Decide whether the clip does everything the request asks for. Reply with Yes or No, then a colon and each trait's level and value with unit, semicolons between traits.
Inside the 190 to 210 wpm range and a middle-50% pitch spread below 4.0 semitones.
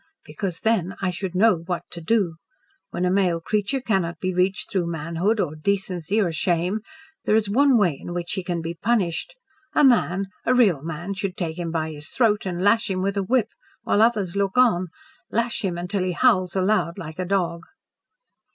Yes: average, 195 wpm; average, 3.3 semitones